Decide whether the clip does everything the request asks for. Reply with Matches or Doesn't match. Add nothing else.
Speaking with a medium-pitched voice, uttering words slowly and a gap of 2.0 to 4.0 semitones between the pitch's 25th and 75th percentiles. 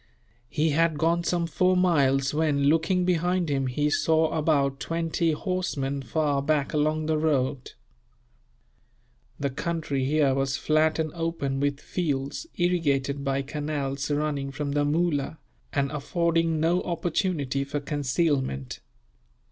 Matches